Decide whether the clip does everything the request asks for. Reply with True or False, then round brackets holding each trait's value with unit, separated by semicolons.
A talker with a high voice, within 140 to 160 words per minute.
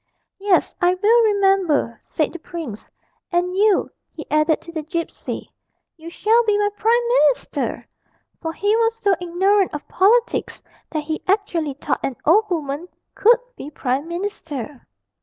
True (350 Hz; 150 wpm)